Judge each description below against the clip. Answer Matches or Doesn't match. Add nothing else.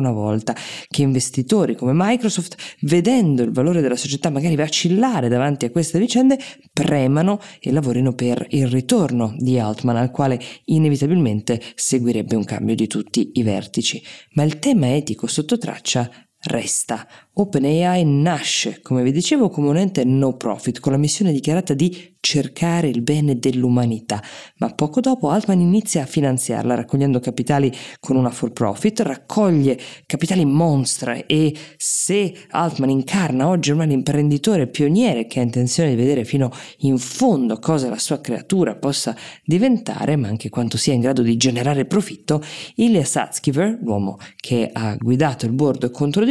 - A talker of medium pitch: Matches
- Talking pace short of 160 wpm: Matches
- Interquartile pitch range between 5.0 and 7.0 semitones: Matches